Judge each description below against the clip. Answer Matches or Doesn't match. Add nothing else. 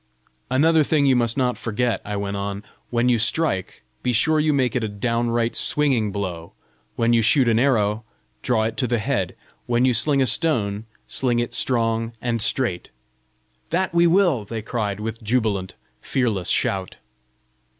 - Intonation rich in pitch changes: Doesn't match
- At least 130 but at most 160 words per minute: Doesn't match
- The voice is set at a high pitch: Doesn't match